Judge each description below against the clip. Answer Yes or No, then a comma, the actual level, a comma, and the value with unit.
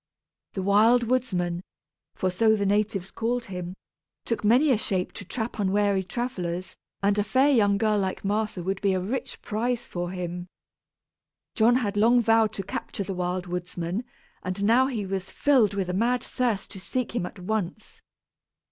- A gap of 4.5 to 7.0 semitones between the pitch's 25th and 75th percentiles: No, average, 3.8 semitones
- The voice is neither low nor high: No, high, 205 Hz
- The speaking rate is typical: Yes, average, 175 wpm